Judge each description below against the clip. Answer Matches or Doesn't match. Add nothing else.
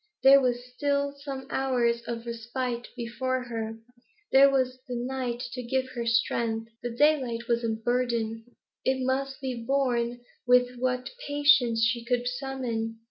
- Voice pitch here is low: Doesn't match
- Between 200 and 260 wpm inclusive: Doesn't match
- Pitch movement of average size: Doesn't match